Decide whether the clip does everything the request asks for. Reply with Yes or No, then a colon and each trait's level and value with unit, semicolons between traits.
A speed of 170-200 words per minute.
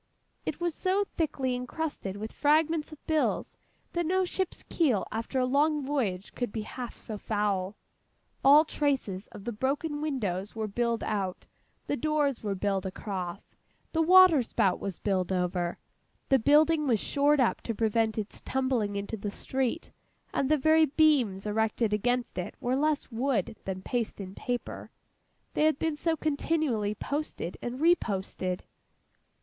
No: average, 155 wpm